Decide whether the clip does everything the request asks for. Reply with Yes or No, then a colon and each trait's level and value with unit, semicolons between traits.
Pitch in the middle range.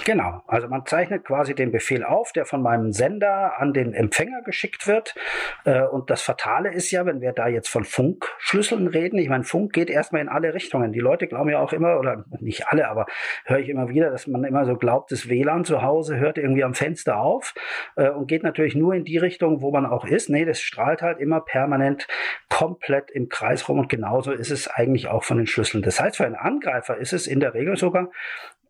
Yes: medium, 145 Hz